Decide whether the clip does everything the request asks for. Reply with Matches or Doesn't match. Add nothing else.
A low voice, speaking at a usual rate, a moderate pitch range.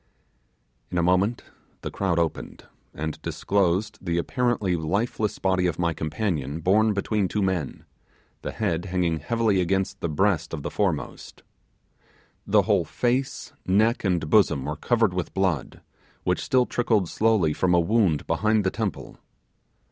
Matches